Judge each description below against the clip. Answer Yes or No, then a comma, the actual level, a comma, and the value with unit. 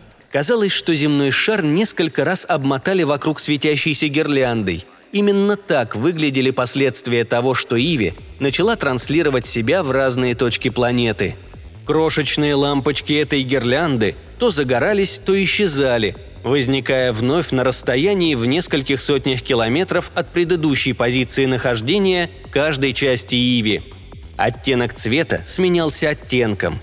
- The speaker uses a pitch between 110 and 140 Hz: Yes, low, 135 Hz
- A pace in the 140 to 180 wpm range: No, average, 115 wpm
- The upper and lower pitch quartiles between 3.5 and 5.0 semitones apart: Yes, average, 4.2 semitones